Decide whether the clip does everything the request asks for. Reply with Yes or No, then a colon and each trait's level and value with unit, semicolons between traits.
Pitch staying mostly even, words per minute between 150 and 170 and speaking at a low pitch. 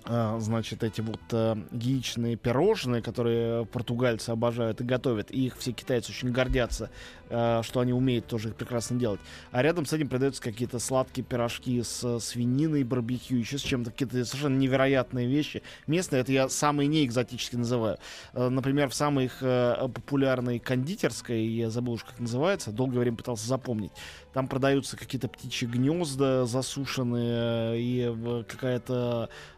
Yes: narrow, 2.0 semitones; average, 155 wpm; low, 125 Hz